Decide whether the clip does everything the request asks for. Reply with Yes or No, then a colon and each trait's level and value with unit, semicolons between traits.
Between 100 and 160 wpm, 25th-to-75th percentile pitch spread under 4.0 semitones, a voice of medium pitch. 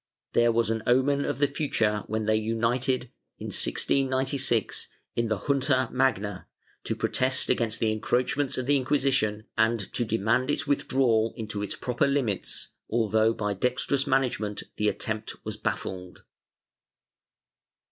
No: average, 140 wpm; average, 3.3 semitones; low, 120 Hz